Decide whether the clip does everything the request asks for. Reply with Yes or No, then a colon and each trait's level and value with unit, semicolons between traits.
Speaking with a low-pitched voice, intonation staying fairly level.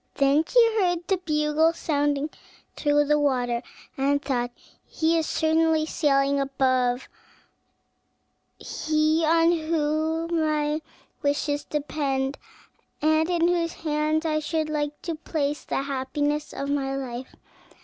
No: very high, 300 Hz; narrow, 2.2 semitones